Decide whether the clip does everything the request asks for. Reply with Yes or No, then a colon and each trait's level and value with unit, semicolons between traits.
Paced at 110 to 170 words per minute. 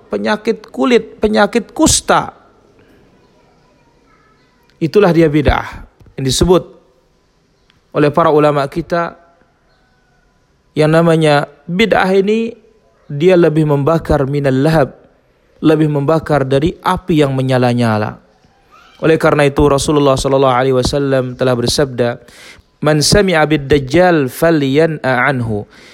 No: average, 95 wpm